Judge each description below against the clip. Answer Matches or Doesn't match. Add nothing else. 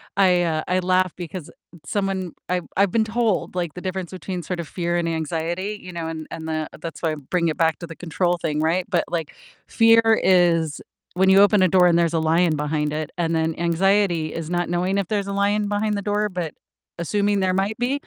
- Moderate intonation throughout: Matches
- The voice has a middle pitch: Matches